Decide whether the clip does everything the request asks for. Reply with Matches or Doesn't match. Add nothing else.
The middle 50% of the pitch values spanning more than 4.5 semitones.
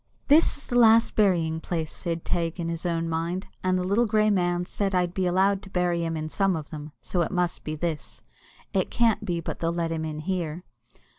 Doesn't match